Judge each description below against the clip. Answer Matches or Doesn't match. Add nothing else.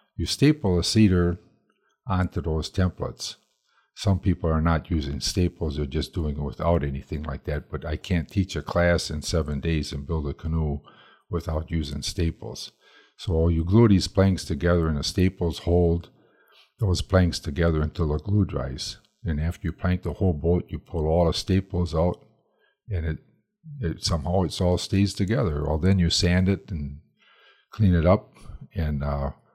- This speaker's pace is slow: Doesn't match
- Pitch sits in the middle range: Doesn't match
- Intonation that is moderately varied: Matches